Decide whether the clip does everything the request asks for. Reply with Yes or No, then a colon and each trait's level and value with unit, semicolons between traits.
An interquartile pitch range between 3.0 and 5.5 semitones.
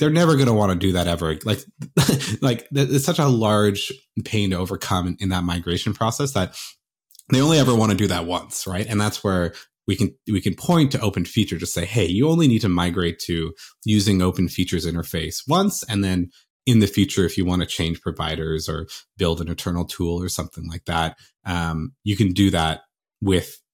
Yes: average, 4.2 semitones